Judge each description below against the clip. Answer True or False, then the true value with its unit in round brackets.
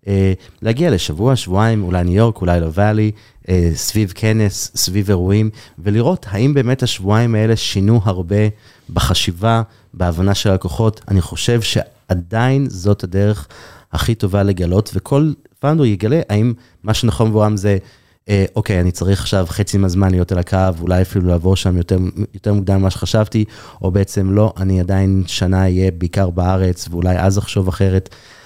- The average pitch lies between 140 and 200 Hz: False (100 Hz)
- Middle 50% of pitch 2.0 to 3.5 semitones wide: True (2.8 semitones)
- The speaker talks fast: True (155 wpm)